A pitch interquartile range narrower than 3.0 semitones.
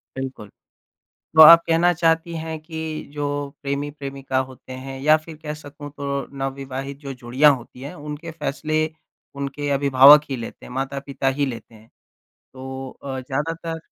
Yes: narrow, 2.4 semitones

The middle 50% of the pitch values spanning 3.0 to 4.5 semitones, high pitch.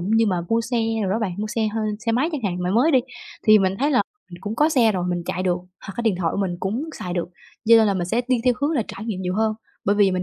Yes: average, 3.9 semitones; high, 215 Hz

